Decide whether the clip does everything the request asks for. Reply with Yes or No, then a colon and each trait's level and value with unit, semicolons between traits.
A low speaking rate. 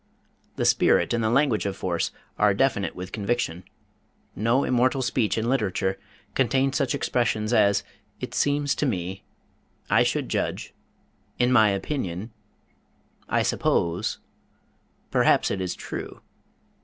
Yes: slow, 130 wpm